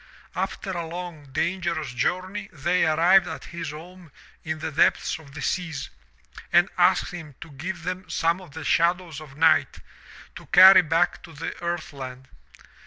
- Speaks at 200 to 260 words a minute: No, average, 165 wpm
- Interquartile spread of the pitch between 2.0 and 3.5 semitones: Yes, average, 2.7 semitones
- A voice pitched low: No, medium, 165 Hz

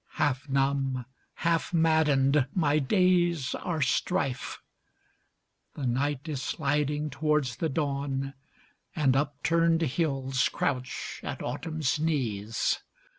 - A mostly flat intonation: No, average, 3.0 semitones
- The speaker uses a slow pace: Yes, slow, 100 wpm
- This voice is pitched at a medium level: Yes, medium, 145 Hz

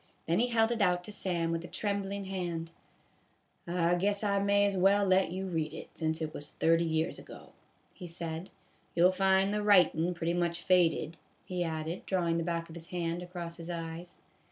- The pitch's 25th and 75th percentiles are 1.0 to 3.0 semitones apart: Yes, narrow, 2.6 semitones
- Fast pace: Yes, fast, 230 wpm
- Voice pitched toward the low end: No, medium, 175 Hz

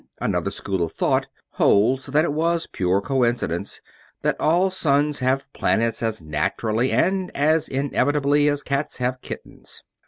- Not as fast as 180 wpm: Yes, average, 145 wpm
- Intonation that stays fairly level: No, average, 4.4 semitones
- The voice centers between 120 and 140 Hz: Yes, low, 135 Hz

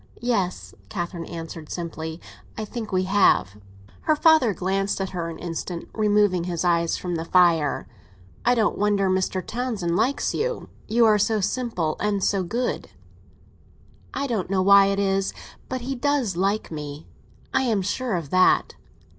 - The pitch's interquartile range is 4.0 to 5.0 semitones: Yes, average, 4.3 semitones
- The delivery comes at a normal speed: Yes, average, 155 wpm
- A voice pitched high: Yes, high, 195 Hz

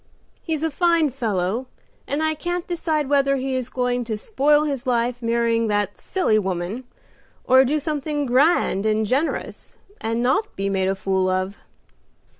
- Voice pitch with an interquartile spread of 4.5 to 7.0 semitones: Yes, wide, 5.6 semitones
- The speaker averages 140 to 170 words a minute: Yes, average, 165 wpm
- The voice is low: No, very high, 255 Hz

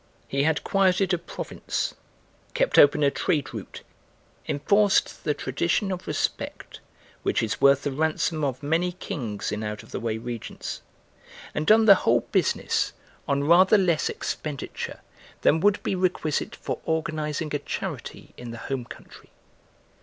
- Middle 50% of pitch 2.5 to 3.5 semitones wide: No, average, 4.7 semitones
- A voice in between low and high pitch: Yes, medium, 155 Hz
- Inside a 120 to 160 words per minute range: Yes, average, 150 wpm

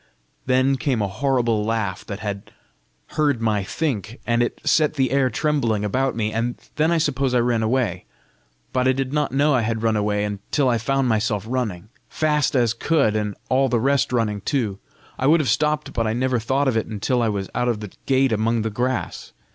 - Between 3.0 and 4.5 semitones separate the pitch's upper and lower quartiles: Yes, average, 3.9 semitones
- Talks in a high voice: No, low, 120 Hz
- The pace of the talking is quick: Yes, fast, 210 wpm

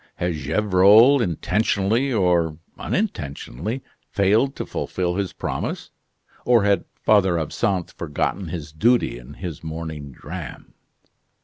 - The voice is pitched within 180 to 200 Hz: No, very low, 90 Hz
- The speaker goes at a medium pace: No, slow, 110 wpm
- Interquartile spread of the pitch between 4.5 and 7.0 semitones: Yes, average, 5.1 semitones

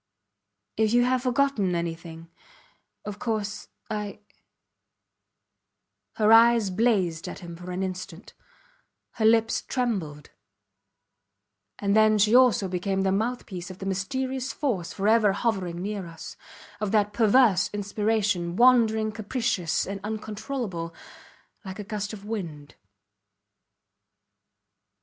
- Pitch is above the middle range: Yes, high, 210 Hz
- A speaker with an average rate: No, slow, 115 wpm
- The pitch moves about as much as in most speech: Yes, average, 3.5 semitones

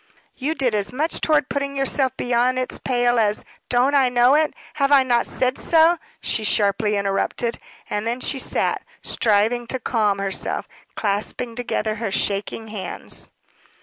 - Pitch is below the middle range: No, high, 245 Hz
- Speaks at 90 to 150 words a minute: No, average, 160 wpm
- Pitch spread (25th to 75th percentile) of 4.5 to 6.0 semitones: No, average, 3.9 semitones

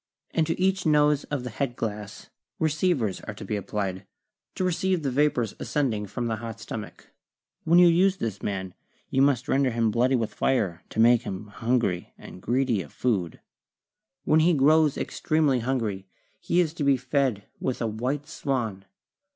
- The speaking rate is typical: Yes, average, 175 wpm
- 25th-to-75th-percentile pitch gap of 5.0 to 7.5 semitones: Yes, wide, 5.6 semitones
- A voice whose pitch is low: Yes, low, 125 Hz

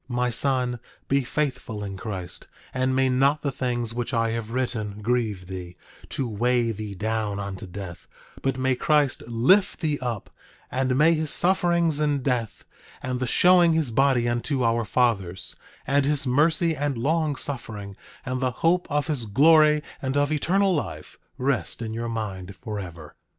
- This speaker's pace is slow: No, average, 165 wpm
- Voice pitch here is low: Yes, low, 125 Hz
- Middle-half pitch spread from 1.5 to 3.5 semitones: No, average, 4.6 semitones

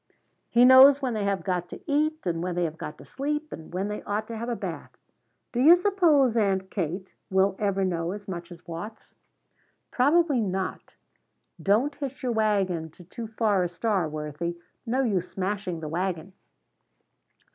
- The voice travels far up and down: Yes, wide, 5.7 semitones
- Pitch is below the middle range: No, high, 200 Hz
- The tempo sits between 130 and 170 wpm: No, average, 180 wpm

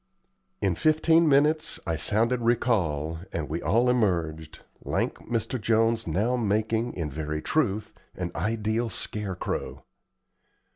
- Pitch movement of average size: No, wide, 6.2 semitones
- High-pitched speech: No, low, 110 Hz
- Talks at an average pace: No, slow, 115 wpm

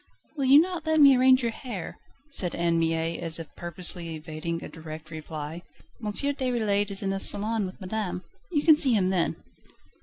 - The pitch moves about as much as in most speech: No, wide, 7.3 semitones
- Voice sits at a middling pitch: No, high, 195 Hz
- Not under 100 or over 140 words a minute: No, average, 185 wpm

